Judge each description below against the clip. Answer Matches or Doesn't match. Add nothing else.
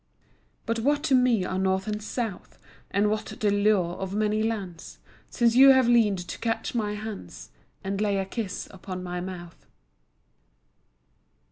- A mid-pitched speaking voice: Doesn't match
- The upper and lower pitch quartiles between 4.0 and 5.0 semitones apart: Doesn't match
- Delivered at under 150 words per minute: Doesn't match